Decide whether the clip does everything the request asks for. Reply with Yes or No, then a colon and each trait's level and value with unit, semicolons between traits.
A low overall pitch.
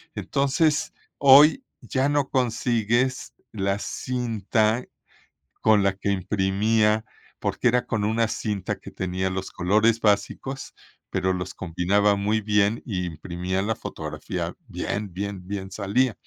Yes: low, 105 Hz